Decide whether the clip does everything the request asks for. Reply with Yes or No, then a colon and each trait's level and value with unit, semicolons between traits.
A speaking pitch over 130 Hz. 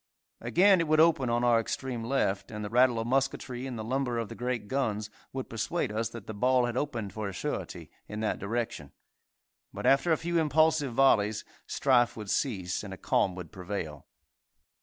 No: low, 120 Hz